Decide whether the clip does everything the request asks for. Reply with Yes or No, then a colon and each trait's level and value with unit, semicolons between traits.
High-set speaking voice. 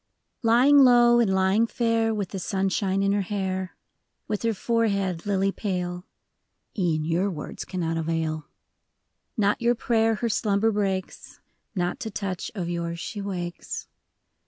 Yes: high, 195 Hz